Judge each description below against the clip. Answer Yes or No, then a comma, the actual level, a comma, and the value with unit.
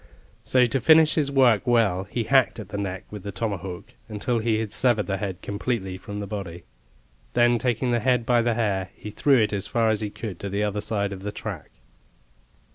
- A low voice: Yes, low, 105 Hz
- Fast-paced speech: Yes, fast, 215 wpm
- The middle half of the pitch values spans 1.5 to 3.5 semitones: Yes, average, 3.2 semitones